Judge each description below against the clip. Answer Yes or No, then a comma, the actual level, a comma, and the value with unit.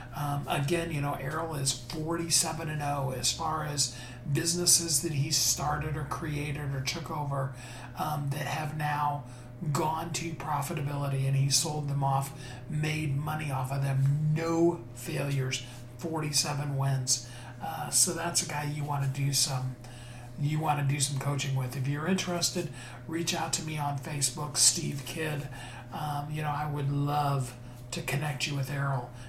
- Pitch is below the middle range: No, medium, 145 Hz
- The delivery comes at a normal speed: Yes, average, 165 wpm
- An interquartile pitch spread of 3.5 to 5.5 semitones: No, narrow, 2.5 semitones